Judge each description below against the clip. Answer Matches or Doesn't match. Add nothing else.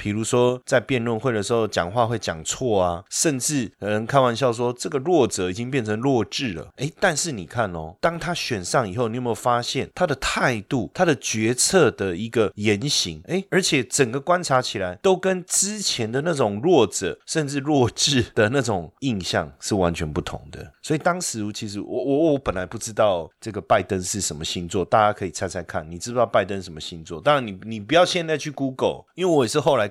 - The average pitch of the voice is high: Doesn't match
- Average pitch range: Doesn't match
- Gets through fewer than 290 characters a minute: Doesn't match